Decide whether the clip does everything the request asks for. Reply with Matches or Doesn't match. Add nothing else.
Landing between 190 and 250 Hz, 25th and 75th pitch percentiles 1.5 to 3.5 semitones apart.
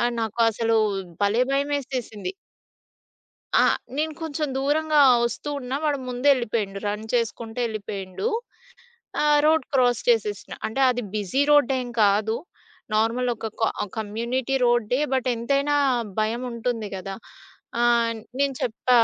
Doesn't match